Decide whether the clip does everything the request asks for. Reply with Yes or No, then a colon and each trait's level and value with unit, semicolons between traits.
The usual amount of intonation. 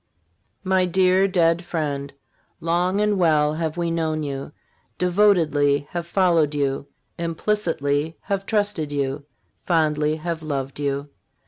Yes: average, 3.7 semitones